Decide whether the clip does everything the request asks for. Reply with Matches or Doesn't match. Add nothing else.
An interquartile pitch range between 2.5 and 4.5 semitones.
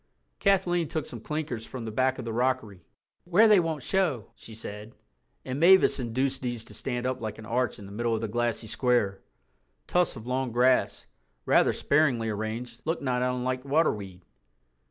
Matches